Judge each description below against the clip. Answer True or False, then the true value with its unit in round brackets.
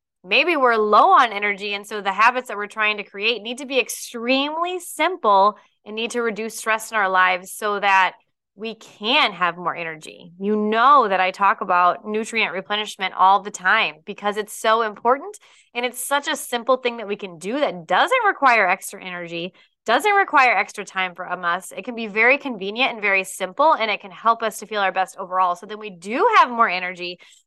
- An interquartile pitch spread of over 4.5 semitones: False (4.0 semitones)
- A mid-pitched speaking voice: False (210 Hz)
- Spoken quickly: True (210 wpm)